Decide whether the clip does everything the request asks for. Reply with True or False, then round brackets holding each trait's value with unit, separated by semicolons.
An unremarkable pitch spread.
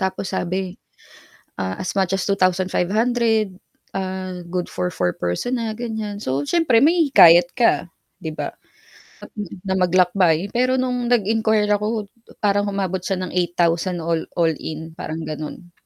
True (4.0 semitones)